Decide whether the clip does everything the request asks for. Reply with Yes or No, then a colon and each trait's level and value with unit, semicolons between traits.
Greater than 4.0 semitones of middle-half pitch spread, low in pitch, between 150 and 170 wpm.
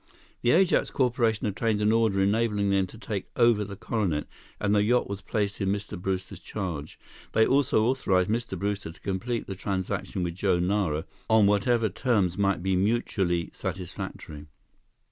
No: average, 3.0 semitones; low, 100 Hz; average, 165 wpm